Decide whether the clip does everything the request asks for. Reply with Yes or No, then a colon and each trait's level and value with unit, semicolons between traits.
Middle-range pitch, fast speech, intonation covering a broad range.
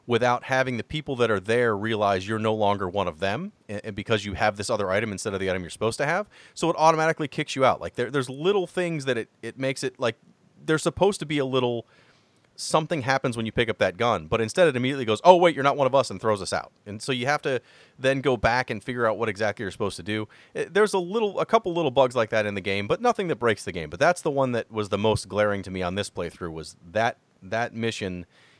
No: low, 120 Hz; fast, 270 wpm; wide, 5.7 semitones